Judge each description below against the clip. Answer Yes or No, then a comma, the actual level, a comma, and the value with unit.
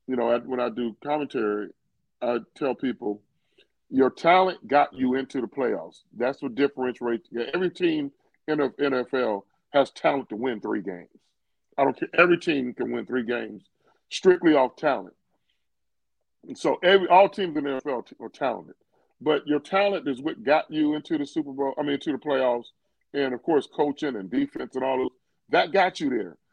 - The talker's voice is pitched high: No, medium, 140 Hz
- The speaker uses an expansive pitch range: Yes, wide, 6.8 semitones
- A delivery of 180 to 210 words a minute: Yes, average, 185 wpm